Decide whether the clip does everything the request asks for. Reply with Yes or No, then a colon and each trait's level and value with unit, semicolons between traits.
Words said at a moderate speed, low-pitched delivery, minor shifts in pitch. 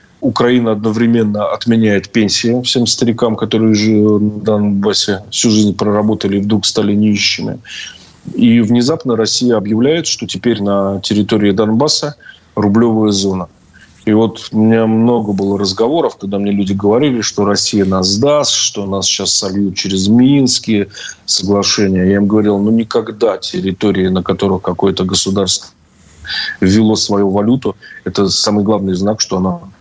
Yes: average, 140 wpm; low, 105 Hz; narrow, 2.2 semitones